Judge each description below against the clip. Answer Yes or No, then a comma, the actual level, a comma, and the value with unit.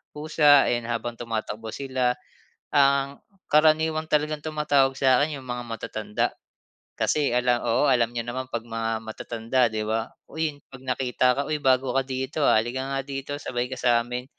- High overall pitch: No, low, 130 Hz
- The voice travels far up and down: No, average, 3.2 semitones